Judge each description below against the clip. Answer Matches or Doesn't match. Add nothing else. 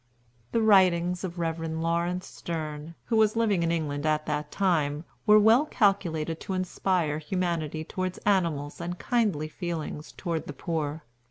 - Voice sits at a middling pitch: Matches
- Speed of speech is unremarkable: Matches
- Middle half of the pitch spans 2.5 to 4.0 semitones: Matches